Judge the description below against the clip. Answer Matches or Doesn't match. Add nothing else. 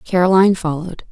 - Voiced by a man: Doesn't match